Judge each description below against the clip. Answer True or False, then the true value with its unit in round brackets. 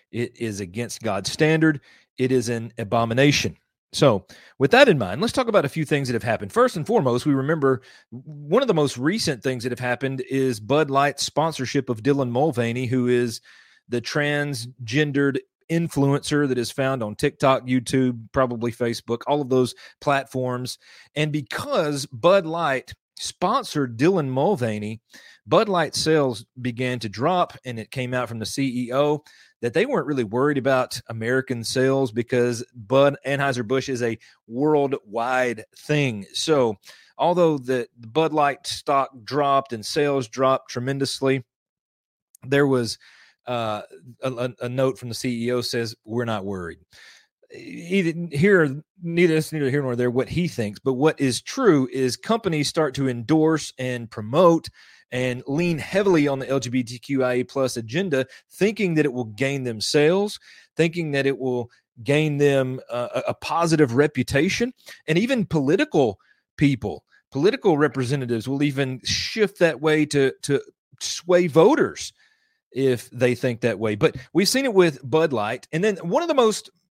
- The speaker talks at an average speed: True (155 wpm)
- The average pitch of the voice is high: False (135 Hz)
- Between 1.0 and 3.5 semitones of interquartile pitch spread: False (3.9 semitones)